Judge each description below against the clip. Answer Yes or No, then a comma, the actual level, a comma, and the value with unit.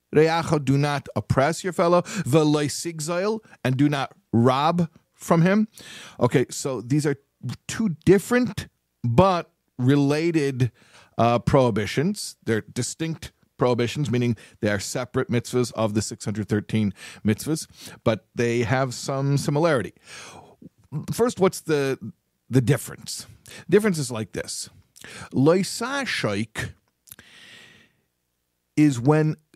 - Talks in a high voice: No, medium, 140 Hz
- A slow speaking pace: Yes, slow, 105 wpm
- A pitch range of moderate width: No, wide, 5.7 semitones